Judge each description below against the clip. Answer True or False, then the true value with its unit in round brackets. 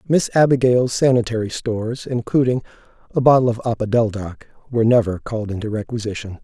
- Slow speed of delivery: True (130 wpm)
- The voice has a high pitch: False (115 Hz)